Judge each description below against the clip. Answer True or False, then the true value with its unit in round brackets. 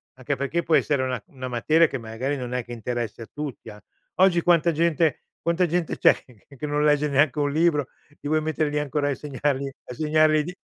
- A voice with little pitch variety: False (3.3 semitones)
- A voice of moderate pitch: True (145 Hz)